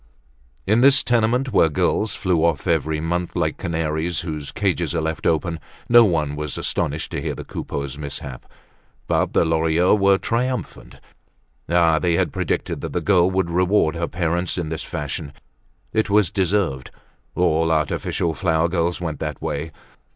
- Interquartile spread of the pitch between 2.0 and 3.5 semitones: Yes, average, 3.0 semitones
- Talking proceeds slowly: No, average, 165 wpm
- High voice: No, very low, 85 Hz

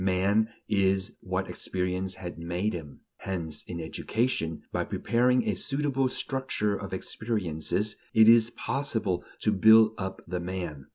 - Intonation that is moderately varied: Yes, average, 3.8 semitones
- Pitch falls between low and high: No, very low, 95 Hz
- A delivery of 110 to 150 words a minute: Yes, slow, 135 wpm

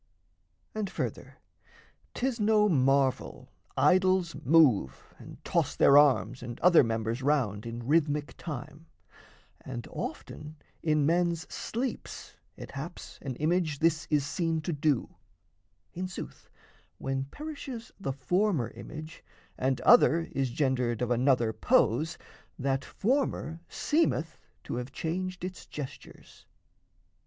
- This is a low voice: No, medium, 150 Hz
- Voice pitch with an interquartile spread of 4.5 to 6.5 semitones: Yes, average, 5.2 semitones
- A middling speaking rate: No, slow, 120 wpm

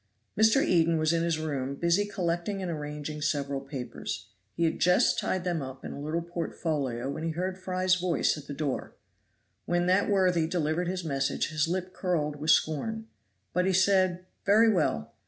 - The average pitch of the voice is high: No, medium, 170 Hz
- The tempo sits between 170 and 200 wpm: Yes, average, 180 wpm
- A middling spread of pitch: Yes, average, 3.6 semitones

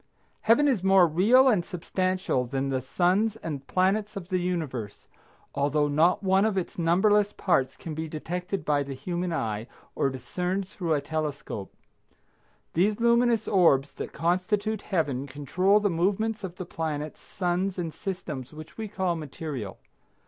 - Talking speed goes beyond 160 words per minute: No, average, 155 wpm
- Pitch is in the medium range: Yes, medium, 175 Hz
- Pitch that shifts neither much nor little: Yes, average, 4.8 semitones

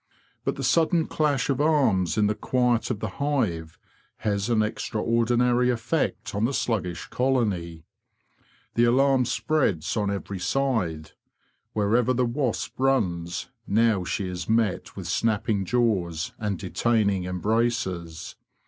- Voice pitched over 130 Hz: No, low, 110 Hz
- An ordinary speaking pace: No, slow, 130 wpm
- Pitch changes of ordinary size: Yes, average, 4.9 semitones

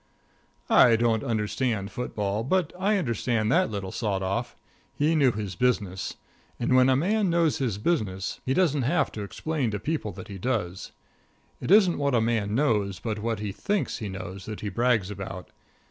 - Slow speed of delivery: No, average, 180 wpm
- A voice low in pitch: Yes, low, 115 Hz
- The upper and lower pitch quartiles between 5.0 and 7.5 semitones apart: Yes, wide, 5.6 semitones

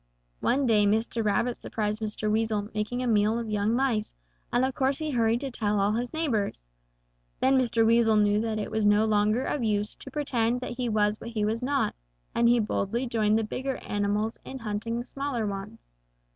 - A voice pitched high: Yes, high, 225 Hz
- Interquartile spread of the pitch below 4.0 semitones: Yes, narrow, 2.6 semitones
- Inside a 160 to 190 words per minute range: No, average, 200 wpm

